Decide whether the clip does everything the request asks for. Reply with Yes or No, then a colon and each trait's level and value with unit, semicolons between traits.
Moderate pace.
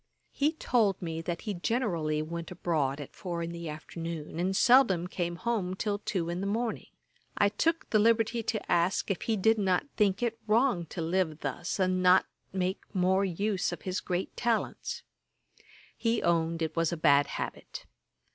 Yes: average, 175 wpm